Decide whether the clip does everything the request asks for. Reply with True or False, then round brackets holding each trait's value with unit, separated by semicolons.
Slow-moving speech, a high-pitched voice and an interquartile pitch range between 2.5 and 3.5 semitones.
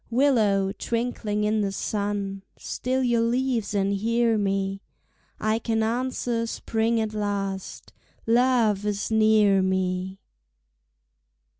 True (110 wpm; 215 Hz; 2.8 semitones)